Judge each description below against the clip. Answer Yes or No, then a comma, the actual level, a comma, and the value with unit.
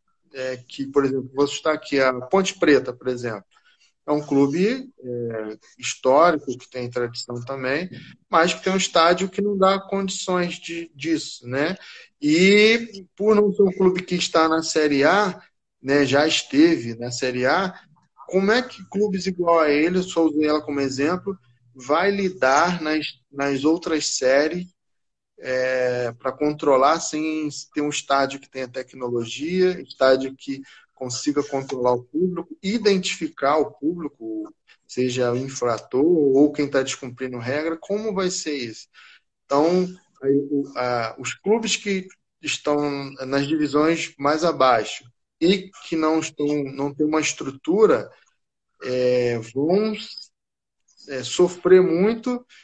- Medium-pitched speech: Yes, medium, 150 Hz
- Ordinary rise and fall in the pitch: No, wide, 5.7 semitones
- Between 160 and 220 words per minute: No, average, 145 wpm